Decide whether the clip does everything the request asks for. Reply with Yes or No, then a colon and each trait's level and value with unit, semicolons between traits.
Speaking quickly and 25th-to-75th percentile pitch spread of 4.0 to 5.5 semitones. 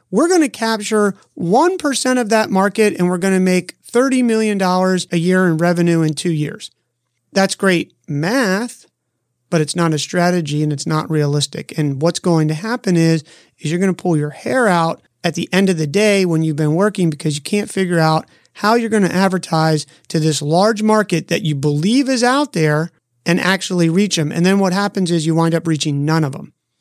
Yes: fast, 210 wpm; average, 4.4 semitones